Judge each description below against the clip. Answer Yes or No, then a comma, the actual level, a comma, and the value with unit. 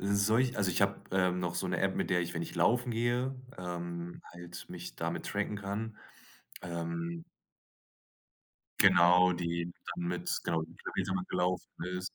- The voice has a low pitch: Yes, very low, 90 Hz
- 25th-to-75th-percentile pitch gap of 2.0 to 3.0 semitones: Yes, average, 2.7 semitones